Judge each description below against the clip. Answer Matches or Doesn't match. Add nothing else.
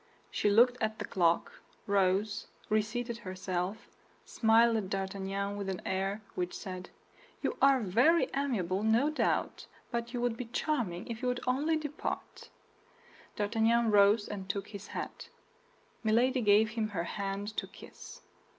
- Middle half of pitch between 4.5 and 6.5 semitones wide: Doesn't match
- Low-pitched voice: Doesn't match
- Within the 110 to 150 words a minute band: Matches